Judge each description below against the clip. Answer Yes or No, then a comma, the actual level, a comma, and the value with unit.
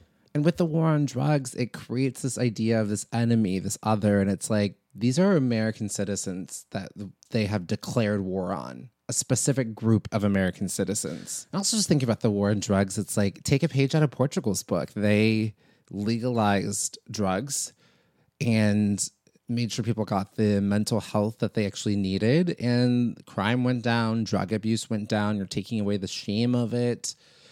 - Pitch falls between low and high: No, low, 110 Hz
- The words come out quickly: No, average, 180 wpm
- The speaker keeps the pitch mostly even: No, average, 3.5 semitones